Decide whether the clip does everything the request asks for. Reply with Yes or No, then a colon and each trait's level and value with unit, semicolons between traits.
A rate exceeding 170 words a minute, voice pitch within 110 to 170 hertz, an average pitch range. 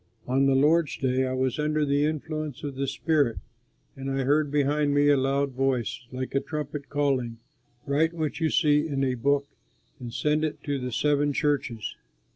No: average, 185 wpm; medium, 140 Hz; narrow, 2.1 semitones